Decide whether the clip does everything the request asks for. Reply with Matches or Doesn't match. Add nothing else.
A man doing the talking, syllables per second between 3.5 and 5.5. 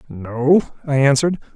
Matches